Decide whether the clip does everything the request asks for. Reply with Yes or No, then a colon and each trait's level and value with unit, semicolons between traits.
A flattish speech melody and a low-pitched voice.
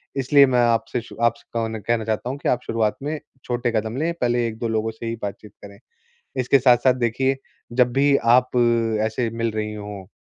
Yes: narrow, 2.3 semitones; low, 115 Hz